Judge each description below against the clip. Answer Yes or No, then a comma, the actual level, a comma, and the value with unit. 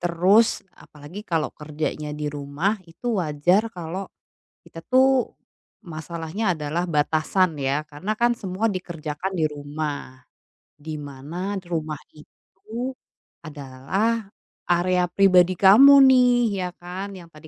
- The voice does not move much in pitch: No, average, 4.3 semitones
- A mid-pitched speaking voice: Yes, medium, 170 Hz